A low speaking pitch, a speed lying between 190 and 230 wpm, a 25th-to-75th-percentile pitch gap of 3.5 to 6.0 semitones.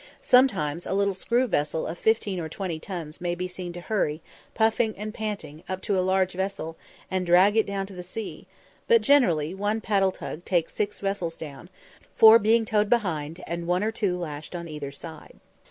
No: medium, 185 Hz; average, 195 wpm; average, 3.8 semitones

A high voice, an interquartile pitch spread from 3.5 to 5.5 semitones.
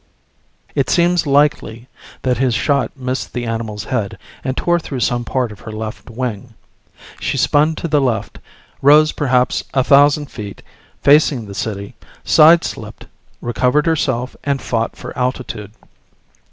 No: low, 130 Hz; average, 4.2 semitones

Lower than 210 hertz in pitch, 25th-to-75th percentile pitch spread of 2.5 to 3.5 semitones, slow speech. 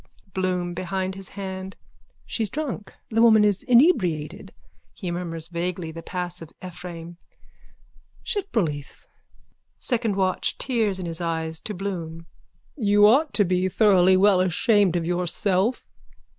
Yes: medium, 185 Hz; average, 3.1 semitones; slow, 130 wpm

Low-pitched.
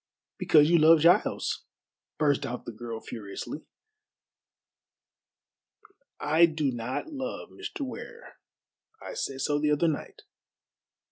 No: medium, 150 Hz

